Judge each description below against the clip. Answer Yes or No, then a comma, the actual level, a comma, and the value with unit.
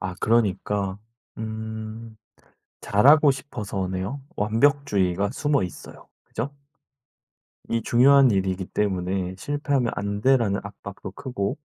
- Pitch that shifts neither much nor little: Yes, average, 4.9 semitones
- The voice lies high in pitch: No, low, 105 Hz